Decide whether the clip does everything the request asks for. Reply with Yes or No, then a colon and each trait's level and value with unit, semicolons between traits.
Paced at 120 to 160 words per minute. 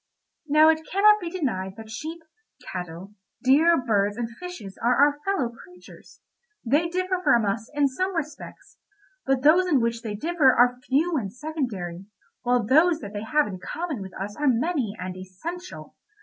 No: average, 170 wpm